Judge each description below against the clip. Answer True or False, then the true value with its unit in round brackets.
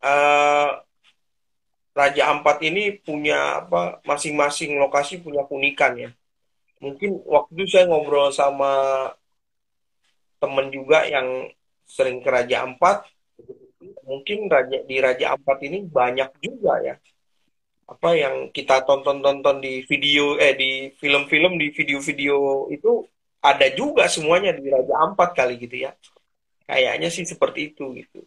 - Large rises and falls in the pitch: False (2.8 semitones)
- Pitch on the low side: False (145 Hz)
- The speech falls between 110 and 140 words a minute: True (125 wpm)